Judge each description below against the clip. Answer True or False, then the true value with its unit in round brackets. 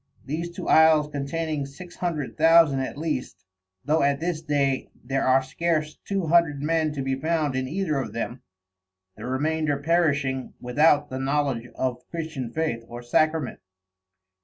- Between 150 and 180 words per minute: True (155 wpm)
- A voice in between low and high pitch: True (150 Hz)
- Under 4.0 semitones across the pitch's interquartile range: True (3.3 semitones)